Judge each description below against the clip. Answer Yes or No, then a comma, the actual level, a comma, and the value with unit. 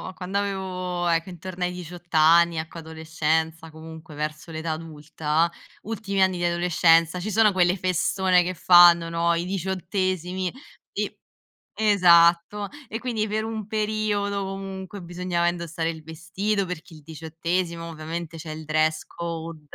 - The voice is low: No, medium, 175 Hz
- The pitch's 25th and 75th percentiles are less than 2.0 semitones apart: No, average, 2.7 semitones